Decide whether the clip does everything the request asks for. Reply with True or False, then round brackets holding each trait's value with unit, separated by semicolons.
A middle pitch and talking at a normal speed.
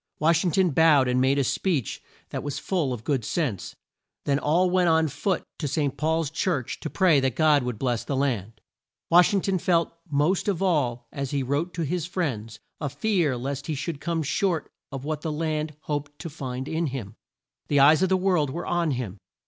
False (150 Hz; 210 wpm)